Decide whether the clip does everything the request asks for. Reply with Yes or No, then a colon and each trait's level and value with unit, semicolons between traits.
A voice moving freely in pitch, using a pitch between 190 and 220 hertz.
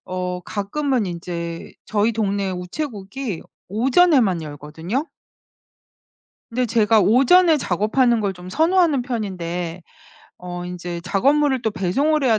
Yes: wide, 6.5 semitones; high, 210 Hz